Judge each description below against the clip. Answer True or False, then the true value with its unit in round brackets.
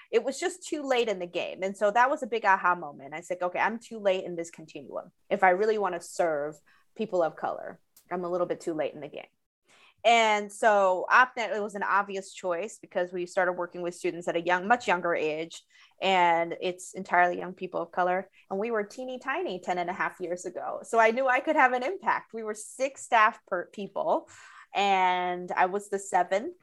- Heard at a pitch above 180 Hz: True (190 Hz)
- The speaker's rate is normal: False (230 wpm)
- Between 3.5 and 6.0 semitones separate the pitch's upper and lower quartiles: True (3.8 semitones)